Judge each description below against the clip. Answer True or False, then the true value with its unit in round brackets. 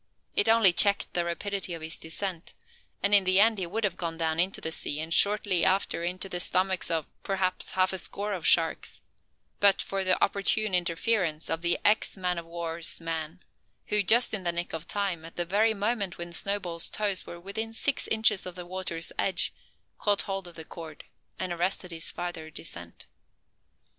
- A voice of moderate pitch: True (180 Hz)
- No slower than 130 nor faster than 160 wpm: False (195 wpm)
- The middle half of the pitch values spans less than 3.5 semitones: True (3.0 semitones)